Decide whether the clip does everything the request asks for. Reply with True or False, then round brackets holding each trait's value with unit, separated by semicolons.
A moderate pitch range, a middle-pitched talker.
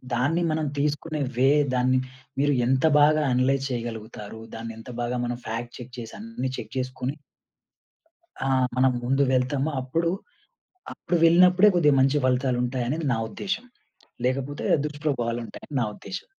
False (3.5 semitones; 130 Hz)